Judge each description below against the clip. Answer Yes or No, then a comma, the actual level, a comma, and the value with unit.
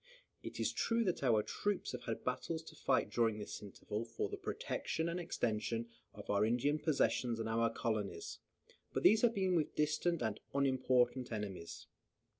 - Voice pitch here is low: Yes, low, 120 Hz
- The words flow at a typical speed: Yes, average, 170 wpm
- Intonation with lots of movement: Yes, wide, 6.2 semitones